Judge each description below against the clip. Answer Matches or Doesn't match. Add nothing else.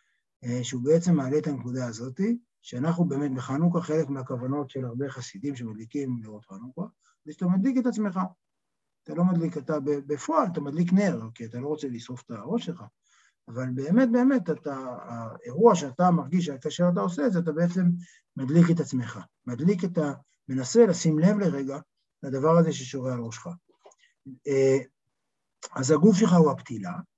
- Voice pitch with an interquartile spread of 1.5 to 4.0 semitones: Doesn't match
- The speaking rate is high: Matches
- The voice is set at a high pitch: Doesn't match